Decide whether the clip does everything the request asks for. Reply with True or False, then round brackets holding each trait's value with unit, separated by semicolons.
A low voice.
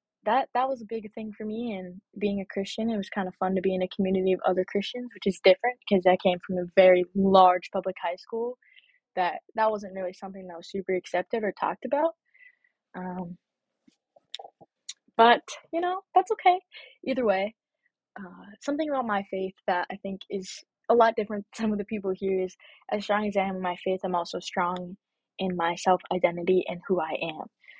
False (200 Hz)